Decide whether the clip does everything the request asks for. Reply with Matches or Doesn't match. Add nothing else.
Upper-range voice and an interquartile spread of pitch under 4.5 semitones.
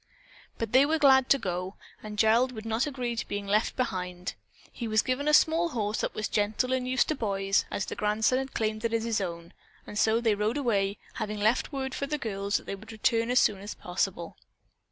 Matches